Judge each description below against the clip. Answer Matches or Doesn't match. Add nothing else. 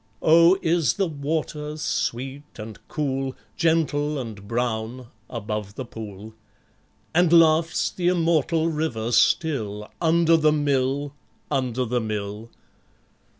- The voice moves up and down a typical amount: Doesn't match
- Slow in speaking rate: Matches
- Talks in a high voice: Doesn't match